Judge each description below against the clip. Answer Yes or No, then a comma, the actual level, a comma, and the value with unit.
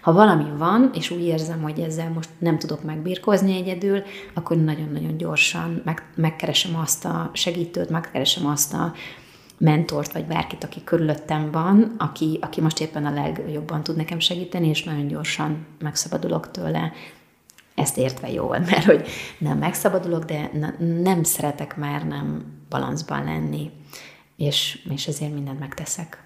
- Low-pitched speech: No, medium, 155 Hz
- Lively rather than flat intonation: No, narrow, 2.5 semitones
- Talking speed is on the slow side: No, average, 145 wpm